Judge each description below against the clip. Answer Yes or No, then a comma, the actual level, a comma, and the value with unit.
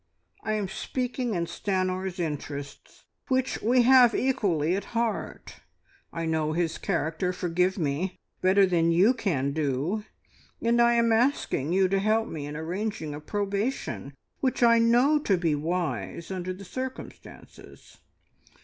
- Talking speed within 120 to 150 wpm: Yes, average, 140 wpm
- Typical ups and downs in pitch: No, wide, 5.9 semitones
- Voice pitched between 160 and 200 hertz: Yes, high, 190 Hz